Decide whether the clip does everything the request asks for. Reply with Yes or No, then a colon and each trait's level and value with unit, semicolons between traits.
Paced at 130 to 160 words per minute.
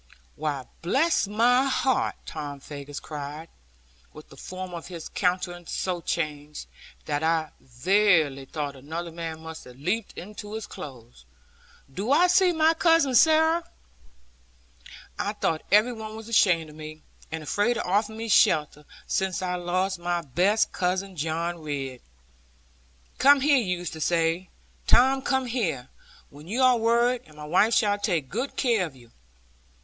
Yes: average, 155 wpm